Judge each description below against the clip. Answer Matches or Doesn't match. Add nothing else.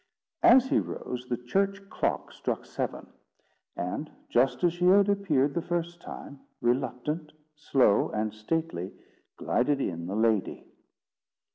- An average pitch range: Doesn't match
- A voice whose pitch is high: Doesn't match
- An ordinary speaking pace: Doesn't match